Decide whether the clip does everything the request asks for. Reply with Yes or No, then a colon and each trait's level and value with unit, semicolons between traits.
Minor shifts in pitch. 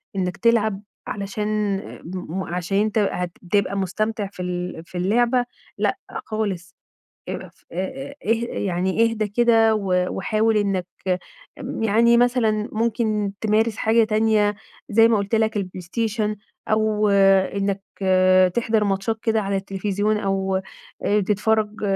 Yes: narrow, 2.3 semitones